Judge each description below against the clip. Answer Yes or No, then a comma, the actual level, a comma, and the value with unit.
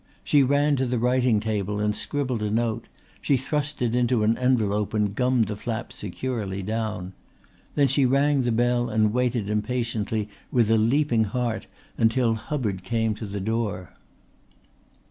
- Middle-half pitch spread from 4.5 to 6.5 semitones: No, average, 3.0 semitones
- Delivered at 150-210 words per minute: Yes, average, 160 wpm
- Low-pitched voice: Yes, low, 115 Hz